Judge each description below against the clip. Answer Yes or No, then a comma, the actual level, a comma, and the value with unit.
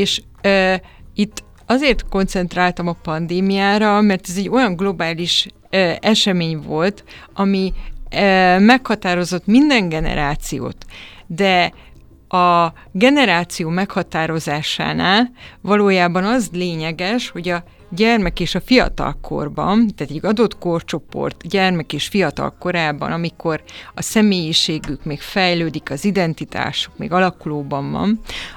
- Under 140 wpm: Yes, average, 110 wpm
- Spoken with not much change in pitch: No, average, 3.3 semitones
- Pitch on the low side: No, medium, 180 Hz